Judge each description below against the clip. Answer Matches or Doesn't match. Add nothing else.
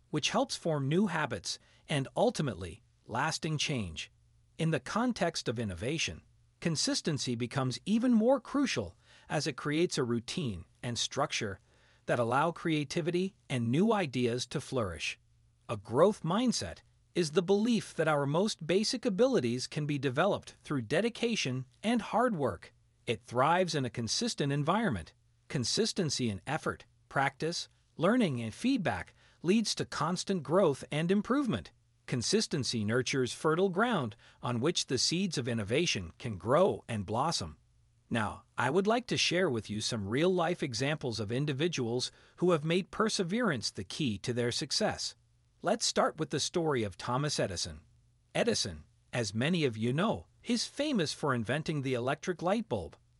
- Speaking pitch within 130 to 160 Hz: Matches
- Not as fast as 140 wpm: Doesn't match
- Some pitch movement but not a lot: Doesn't match